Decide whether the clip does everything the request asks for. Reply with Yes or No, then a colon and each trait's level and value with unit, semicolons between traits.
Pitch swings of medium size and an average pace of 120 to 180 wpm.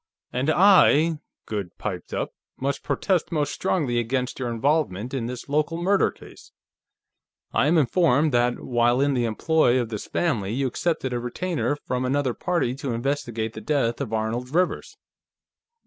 Yes: average, 4.4 semitones; average, 160 wpm